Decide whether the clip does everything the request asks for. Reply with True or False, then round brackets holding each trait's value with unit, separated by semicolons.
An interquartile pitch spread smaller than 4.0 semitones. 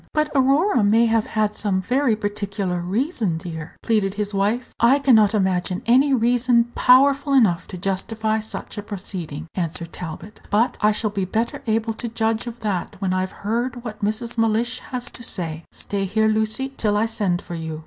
True (3.6 semitones)